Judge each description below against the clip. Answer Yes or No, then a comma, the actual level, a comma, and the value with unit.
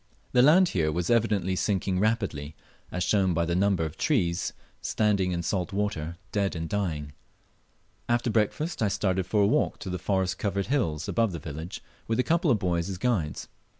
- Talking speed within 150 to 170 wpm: No, average, 185 wpm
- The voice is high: No, very low, 95 Hz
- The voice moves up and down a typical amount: Yes, average, 4.0 semitones